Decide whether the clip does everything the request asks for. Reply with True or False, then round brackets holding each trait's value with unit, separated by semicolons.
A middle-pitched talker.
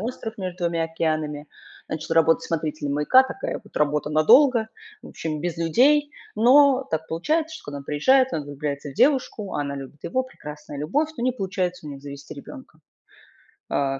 True (165 Hz)